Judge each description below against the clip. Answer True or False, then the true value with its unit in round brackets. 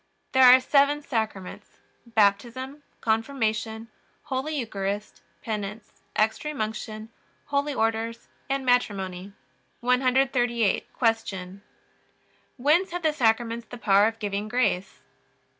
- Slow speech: True (100 wpm)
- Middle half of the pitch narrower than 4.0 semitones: True (3.6 semitones)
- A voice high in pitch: True (230 Hz)